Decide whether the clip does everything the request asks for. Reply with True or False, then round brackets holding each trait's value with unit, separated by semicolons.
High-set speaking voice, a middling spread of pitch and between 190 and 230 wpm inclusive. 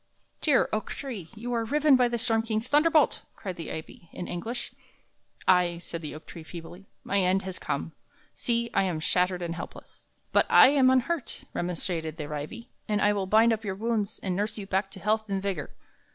True (200 Hz; 4.7 semitones; 200 wpm)